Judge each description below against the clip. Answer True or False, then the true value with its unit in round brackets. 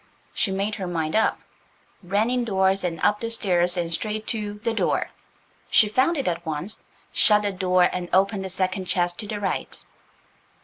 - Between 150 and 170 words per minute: True (165 wpm)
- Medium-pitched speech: False (195 Hz)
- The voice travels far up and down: False (3.0 semitones)